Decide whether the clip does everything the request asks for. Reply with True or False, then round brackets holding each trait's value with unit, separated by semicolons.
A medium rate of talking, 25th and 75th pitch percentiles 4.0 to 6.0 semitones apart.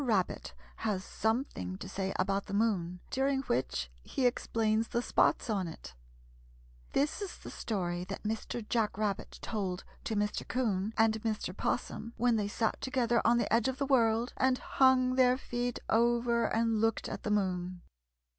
False (165 wpm; 3.5 semitones)